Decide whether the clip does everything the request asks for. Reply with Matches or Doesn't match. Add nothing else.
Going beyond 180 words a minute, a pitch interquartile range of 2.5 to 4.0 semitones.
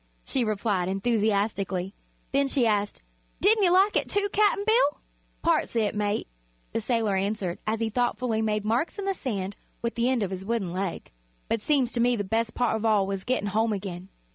Matches